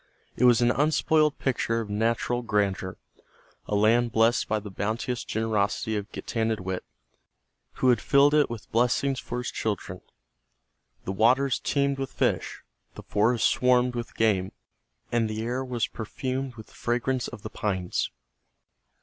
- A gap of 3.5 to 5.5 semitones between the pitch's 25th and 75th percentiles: No, average, 2.8 semitones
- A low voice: Yes, low, 115 Hz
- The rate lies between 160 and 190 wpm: No, average, 150 wpm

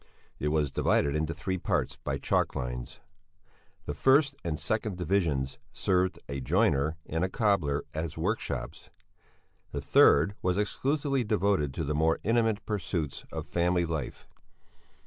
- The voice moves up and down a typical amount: No, wide, 5.7 semitones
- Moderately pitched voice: No, very low, 85 Hz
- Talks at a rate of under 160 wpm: Yes, average, 140 wpm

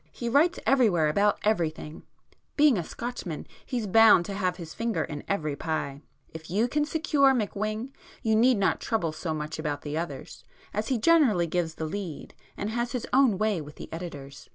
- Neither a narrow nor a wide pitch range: No, wide, 6.9 semitones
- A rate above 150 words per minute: Yes, average, 180 wpm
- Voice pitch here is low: No, high, 200 Hz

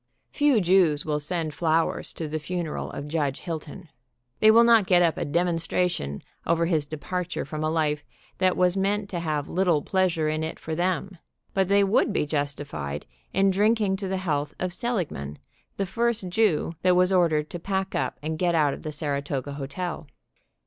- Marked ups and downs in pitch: No, average, 3.9 semitones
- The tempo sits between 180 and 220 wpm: Yes, average, 185 wpm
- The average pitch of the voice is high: No, medium, 170 Hz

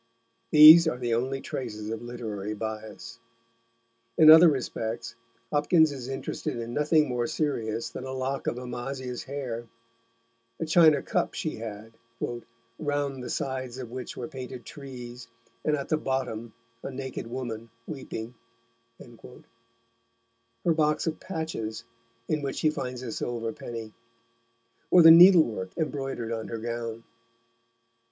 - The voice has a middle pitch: No, low, 125 Hz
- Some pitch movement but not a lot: Yes, average, 3.9 semitones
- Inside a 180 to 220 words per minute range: No, slow, 135 wpm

